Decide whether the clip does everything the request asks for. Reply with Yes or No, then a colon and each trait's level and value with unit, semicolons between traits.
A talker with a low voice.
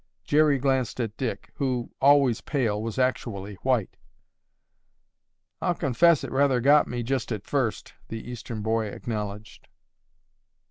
Yes: low, 125 Hz